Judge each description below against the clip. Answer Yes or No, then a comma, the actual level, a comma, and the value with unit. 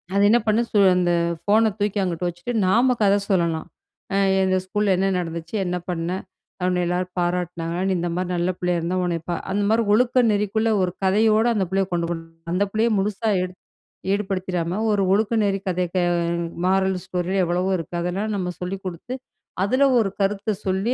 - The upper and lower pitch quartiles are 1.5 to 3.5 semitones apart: Yes, average, 2.8 semitones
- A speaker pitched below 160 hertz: No, high, 190 Hz